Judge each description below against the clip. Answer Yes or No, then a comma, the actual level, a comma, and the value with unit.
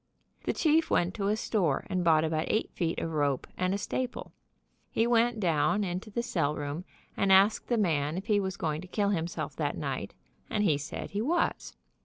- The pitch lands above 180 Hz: Yes, high, 190 Hz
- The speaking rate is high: Yes, fast, 230 wpm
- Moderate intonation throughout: Yes, average, 4.9 semitones